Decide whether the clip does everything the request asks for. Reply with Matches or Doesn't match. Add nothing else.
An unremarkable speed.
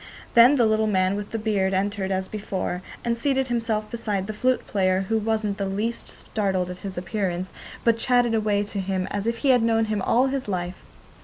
Doesn't match